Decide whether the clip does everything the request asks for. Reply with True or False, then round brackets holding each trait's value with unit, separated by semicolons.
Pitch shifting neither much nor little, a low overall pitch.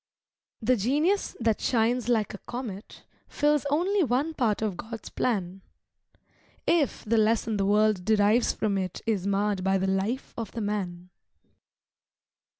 False (3.8 semitones; 220 Hz)